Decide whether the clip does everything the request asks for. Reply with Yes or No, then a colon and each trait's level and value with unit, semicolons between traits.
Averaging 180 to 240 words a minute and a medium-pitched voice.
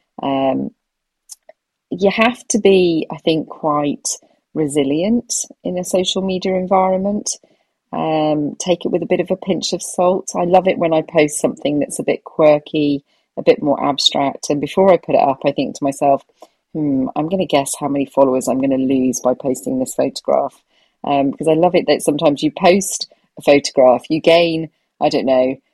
Yes: average, 190 wpm; medium, 160 Hz